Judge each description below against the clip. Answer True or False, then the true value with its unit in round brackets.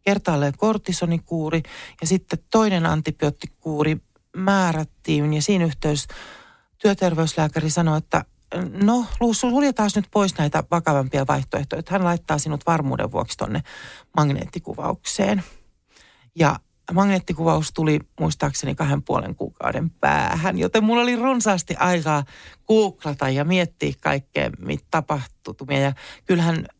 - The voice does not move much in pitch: False (4.4 semitones)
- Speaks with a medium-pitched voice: True (165 Hz)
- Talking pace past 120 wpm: False (105 wpm)